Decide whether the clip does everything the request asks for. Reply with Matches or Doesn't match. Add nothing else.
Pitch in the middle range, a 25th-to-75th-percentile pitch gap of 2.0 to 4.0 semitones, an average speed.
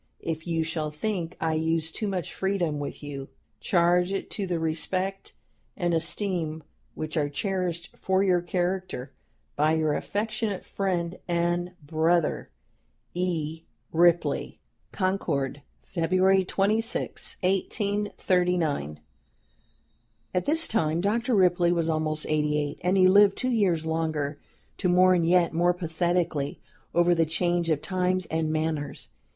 Doesn't match